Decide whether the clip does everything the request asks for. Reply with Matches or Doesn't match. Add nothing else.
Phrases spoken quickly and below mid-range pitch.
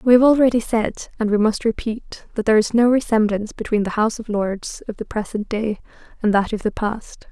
Doesn't match